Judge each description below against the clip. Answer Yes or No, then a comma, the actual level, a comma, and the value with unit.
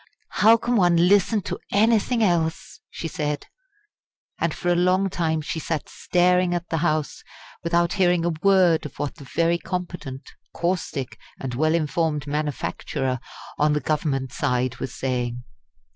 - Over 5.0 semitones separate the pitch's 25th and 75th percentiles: No, average, 3.5 semitones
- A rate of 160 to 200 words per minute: No, average, 150 wpm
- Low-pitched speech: No, medium, 165 Hz